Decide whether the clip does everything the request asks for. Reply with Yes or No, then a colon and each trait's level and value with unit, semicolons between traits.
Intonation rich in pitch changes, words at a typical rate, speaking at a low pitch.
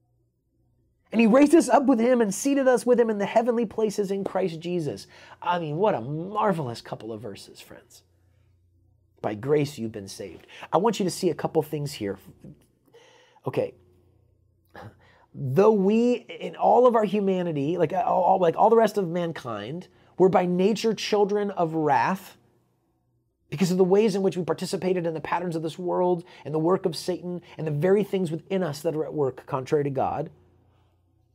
No: wide, 6.6 semitones; average, 185 wpm; medium, 175 Hz